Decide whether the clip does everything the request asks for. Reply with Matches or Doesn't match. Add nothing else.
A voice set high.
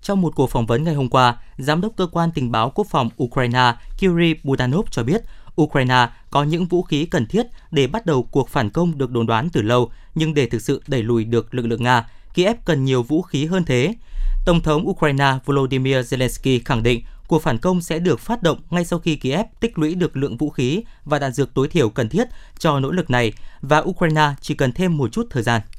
Doesn't match